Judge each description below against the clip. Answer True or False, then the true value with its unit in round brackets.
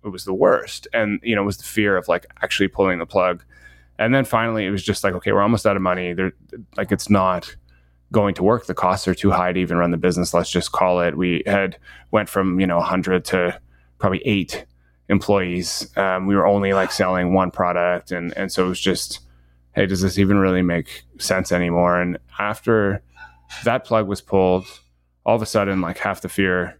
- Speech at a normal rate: False (220 wpm)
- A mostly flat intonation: True (2.1 semitones)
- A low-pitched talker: True (90 Hz)